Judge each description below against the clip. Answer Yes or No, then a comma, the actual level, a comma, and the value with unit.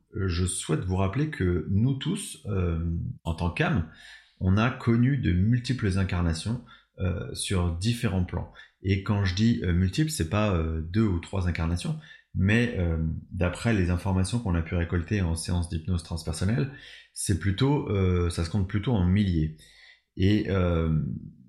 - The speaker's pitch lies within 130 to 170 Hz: No, very low, 95 Hz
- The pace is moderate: Yes, average, 160 wpm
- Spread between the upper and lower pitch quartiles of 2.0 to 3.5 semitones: No, average, 4.1 semitones